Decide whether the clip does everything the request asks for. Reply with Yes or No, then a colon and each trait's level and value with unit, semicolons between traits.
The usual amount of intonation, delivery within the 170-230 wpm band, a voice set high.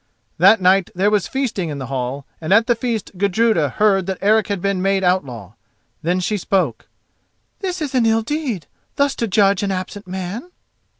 Yes: average, 3.9 semitones; average, 185 wpm; high, 195 Hz